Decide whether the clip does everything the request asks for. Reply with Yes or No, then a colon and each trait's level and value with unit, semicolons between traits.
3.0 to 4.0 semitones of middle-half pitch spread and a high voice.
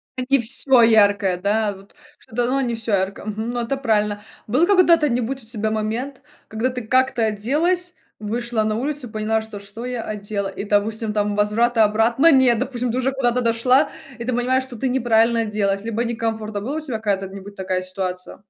Yes: average, 3.3 semitones; high, 225 Hz